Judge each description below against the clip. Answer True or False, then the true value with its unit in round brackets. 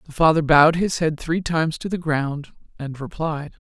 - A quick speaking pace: False (195 wpm)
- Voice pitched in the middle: True (155 Hz)